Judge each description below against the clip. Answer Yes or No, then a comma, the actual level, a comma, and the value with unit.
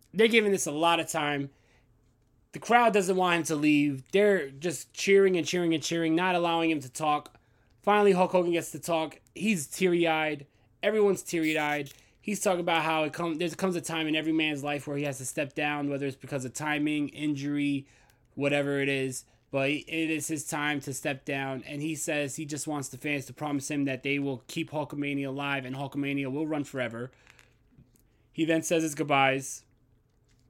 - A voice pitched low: No, medium, 150 Hz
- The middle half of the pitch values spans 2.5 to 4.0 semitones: Yes, average, 3.1 semitones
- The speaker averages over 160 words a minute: Yes, average, 200 wpm